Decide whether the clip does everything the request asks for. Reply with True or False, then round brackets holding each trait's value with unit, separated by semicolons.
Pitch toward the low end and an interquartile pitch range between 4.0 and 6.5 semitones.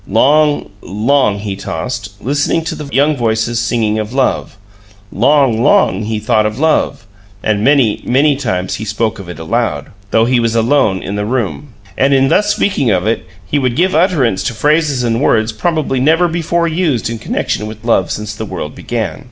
True (120 Hz; 5.0 semitones)